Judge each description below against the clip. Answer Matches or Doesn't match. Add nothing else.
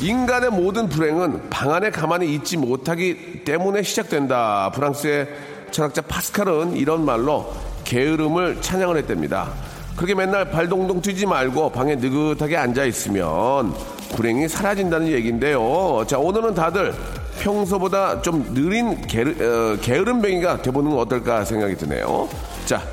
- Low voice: Doesn't match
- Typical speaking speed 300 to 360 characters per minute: Matches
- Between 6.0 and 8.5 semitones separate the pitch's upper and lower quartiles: Matches